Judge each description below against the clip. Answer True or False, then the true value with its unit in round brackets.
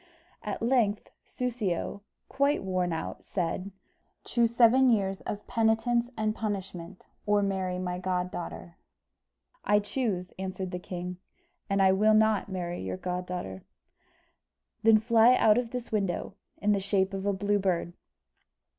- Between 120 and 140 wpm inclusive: True (135 wpm)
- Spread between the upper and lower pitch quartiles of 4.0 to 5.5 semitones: False (3.4 semitones)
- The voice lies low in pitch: False (200 Hz)